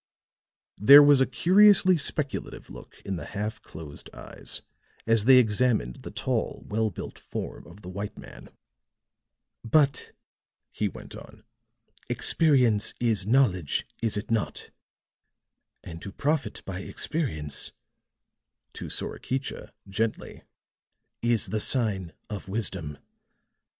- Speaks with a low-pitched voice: Yes, low, 110 Hz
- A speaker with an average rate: No, slow, 115 wpm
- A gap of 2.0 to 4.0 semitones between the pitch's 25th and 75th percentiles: No, wide, 5.4 semitones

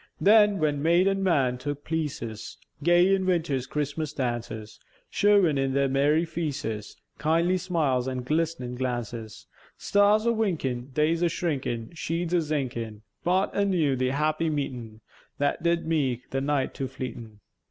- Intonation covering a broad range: No, average, 4.9 semitones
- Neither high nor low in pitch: Yes, medium, 150 Hz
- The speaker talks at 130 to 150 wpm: Yes, average, 145 wpm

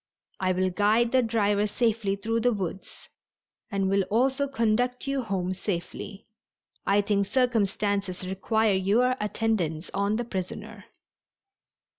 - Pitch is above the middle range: Yes, high, 205 Hz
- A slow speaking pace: Yes, slow, 125 wpm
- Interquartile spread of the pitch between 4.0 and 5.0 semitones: No, average, 3.0 semitones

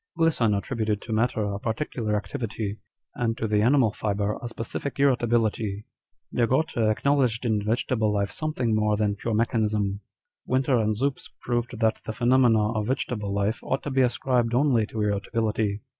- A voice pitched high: No, low, 115 Hz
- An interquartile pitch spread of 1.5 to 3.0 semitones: Yes, average, 2.7 semitones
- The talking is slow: No, average, 160 wpm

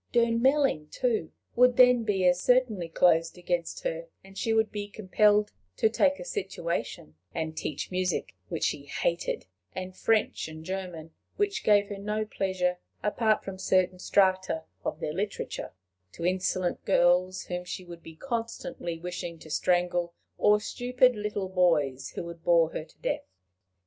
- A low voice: No, medium, 185 Hz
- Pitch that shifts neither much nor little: Yes, average, 4.1 semitones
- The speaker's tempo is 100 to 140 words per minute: No, average, 155 wpm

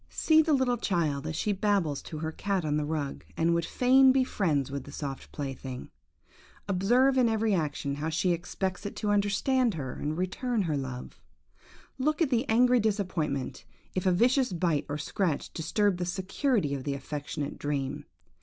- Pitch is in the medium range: Yes, medium, 180 Hz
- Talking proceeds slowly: No, average, 180 wpm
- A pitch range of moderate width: No, wide, 7.1 semitones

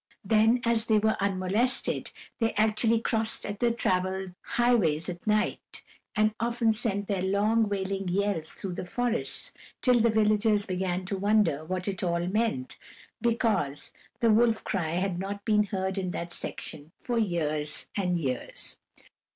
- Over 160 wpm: No, average, 150 wpm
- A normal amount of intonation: Yes, average, 3.5 semitones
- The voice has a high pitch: Yes, high, 200 Hz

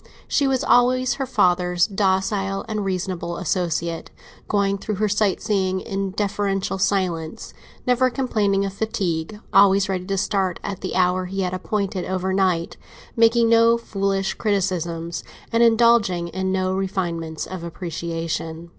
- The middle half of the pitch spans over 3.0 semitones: No, narrow, 2.6 semitones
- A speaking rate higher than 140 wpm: No, slow, 135 wpm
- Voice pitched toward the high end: Yes, high, 195 Hz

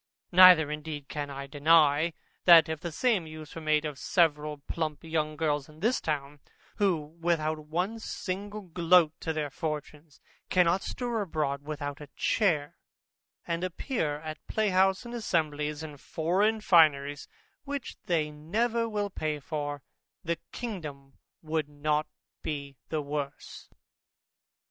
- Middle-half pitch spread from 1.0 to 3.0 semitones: No, average, 3.4 semitones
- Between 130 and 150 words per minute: Yes, average, 140 wpm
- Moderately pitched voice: Yes, medium, 155 Hz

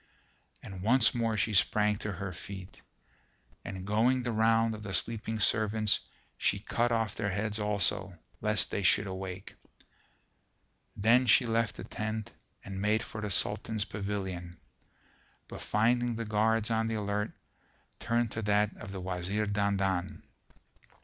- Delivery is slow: No, average, 145 wpm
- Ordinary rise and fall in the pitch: No, narrow, 2.2 semitones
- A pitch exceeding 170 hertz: No, low, 105 Hz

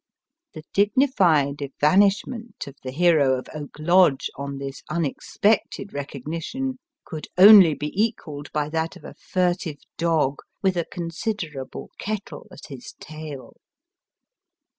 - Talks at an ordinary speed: No, slow, 125 wpm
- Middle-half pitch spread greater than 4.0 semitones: Yes, average, 5.2 semitones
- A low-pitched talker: No, medium, 160 Hz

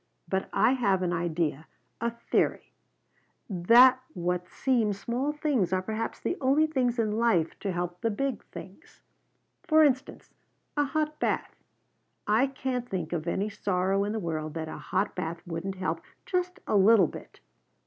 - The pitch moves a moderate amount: No, wide, 6.5 semitones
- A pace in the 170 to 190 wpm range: No, average, 160 wpm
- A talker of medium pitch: No, high, 205 Hz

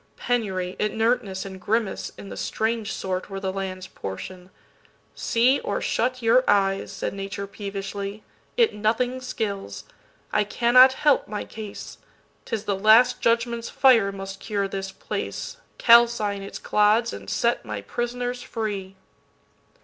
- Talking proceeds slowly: Yes, slow, 125 wpm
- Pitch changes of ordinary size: Yes, average, 3.4 semitones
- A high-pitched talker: Yes, high, 210 Hz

